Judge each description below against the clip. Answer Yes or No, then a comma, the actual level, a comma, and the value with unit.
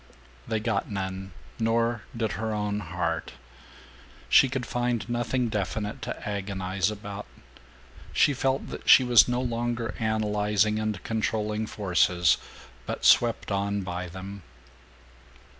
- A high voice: No, low, 105 Hz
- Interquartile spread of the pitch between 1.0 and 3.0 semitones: Yes, average, 2.7 semitones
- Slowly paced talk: Yes, slow, 125 wpm